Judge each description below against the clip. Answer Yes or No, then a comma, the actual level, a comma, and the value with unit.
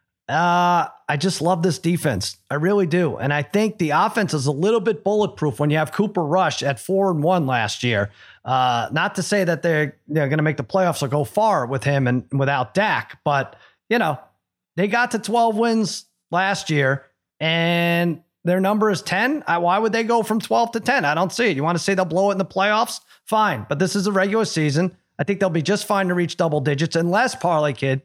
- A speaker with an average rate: No, fast, 230 wpm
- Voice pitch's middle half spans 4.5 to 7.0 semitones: Yes, wide, 5.4 semitones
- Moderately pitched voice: Yes, medium, 175 Hz